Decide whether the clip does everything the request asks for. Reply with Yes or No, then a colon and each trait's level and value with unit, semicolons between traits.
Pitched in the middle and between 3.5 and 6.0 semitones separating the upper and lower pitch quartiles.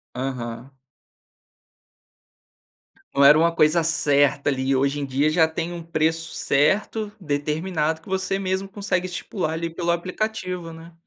Yes: medium, 165 Hz; average, 3.9 semitones